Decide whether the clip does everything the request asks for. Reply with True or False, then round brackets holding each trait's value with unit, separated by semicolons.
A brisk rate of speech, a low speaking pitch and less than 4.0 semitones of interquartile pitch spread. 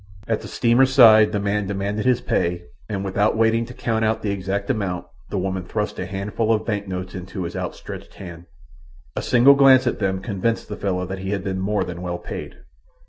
True (210 wpm; 100 Hz; 2.9 semitones)